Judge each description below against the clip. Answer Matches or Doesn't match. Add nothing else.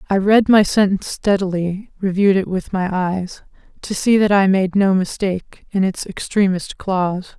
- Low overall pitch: Doesn't match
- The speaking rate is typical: Matches